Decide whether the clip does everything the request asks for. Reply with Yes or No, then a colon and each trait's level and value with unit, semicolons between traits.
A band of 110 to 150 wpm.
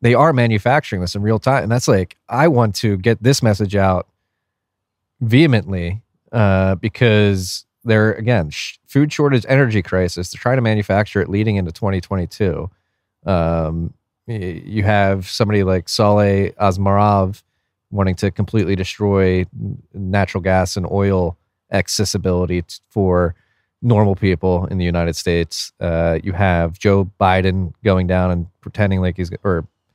Yes: average, 140 wpm